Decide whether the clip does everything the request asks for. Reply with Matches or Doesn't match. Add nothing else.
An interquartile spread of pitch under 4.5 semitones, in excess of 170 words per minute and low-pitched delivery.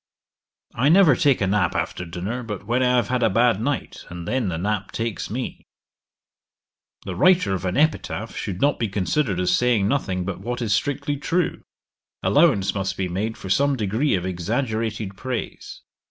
Doesn't match